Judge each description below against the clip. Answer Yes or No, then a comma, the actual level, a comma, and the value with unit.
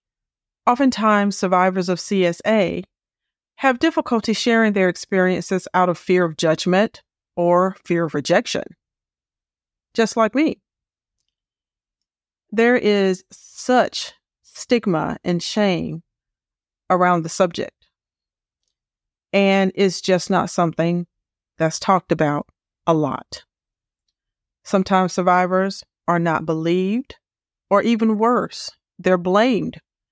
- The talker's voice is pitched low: No, medium, 185 Hz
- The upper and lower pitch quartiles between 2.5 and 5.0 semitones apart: Yes, average, 3.4 semitones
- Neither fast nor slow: No, slow, 100 wpm